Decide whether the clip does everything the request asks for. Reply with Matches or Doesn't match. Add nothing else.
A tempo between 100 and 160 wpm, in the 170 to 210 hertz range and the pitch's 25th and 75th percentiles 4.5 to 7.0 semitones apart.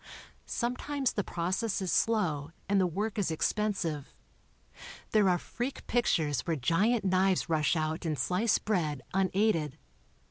Matches